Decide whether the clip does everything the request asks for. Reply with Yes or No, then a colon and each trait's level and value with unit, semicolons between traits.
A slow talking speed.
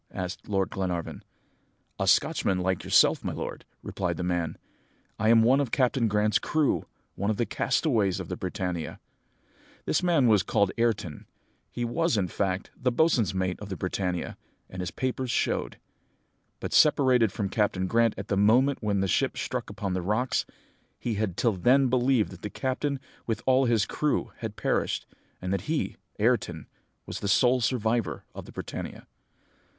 No: average, 170 wpm